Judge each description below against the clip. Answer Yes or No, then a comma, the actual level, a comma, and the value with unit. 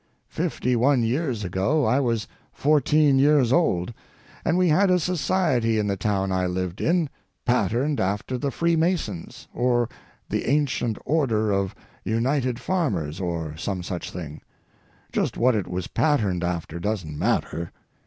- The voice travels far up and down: Yes, wide, 7.7 semitones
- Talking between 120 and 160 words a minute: Yes, average, 140 wpm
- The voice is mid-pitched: No, low, 115 Hz